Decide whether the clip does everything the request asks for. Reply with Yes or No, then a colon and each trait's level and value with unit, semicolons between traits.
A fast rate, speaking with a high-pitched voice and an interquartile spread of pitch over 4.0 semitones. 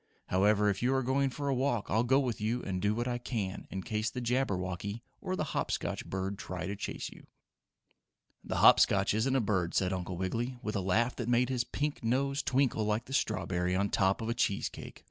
No: fast, 225 wpm; low, 110 Hz; average, 4.6 semitones